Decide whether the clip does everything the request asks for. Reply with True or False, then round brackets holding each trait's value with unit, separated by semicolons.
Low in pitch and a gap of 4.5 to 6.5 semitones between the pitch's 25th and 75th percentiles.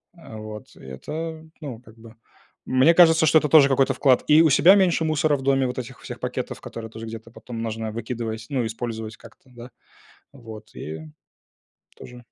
True (125 Hz; 5.0 semitones)